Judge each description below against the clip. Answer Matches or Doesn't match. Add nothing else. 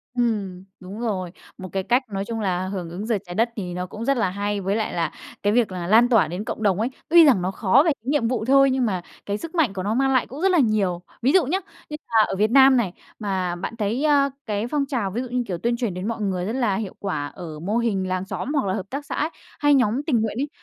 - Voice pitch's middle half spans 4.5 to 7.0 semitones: Matches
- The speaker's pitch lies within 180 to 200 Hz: Doesn't match